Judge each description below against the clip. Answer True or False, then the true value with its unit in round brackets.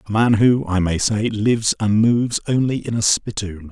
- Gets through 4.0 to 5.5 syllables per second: True (5.0 syllables/s)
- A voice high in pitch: False (110 Hz)